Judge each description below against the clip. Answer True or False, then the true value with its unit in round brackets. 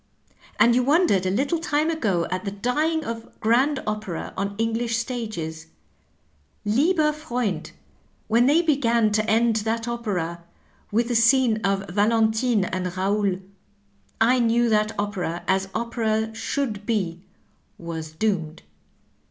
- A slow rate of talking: True (130 wpm)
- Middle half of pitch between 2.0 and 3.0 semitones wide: False (3.6 semitones)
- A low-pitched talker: False (220 Hz)